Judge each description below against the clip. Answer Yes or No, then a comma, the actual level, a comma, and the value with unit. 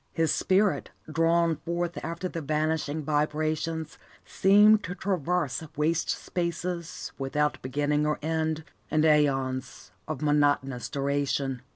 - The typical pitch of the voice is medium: Yes, medium, 155 Hz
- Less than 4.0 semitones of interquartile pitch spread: Yes, narrow, 2.6 semitones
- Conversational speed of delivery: No, slow, 110 wpm